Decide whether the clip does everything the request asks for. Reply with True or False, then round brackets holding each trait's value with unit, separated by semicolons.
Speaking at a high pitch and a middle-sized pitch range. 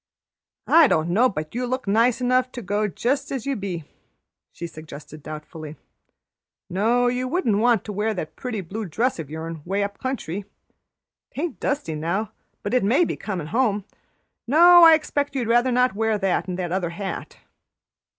False (215 Hz; 6.3 semitones)